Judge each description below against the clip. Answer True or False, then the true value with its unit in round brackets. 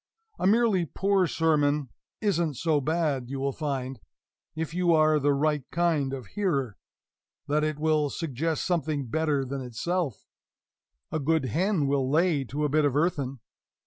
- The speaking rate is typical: True (160 wpm)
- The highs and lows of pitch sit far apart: False (3.3 semitones)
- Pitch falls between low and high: True (150 Hz)